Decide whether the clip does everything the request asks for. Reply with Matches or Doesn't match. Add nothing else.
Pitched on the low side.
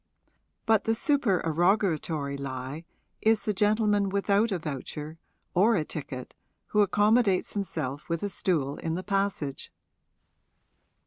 Doesn't match